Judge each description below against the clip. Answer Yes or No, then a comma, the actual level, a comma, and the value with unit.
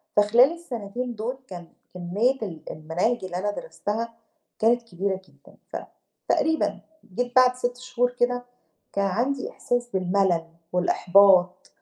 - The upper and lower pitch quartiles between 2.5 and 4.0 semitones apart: No, average, 4.9 semitones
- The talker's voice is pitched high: Yes, high, 220 Hz